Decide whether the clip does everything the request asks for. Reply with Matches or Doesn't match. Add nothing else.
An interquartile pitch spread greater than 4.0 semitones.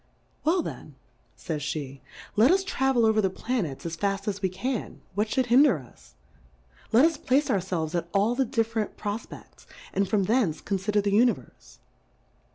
Matches